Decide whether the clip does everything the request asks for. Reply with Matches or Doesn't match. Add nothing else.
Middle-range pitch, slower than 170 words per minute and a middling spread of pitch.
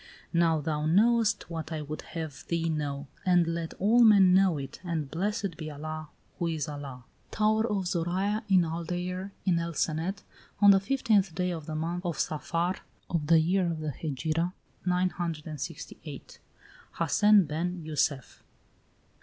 Matches